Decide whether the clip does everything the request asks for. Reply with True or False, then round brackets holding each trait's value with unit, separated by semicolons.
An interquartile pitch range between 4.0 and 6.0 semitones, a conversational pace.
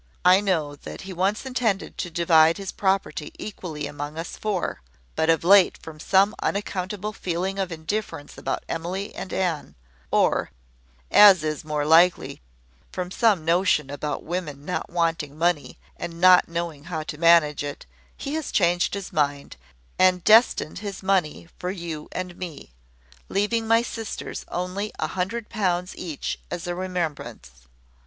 False (3.6 semitones; 150 wpm)